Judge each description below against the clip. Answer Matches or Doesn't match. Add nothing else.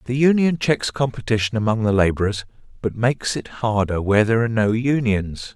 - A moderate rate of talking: Matches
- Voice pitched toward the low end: Matches